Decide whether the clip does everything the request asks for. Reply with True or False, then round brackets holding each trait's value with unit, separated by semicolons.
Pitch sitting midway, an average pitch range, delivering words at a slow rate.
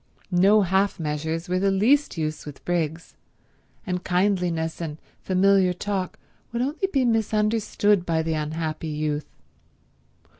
True (180 Hz; 4.0 semitones; 125 wpm)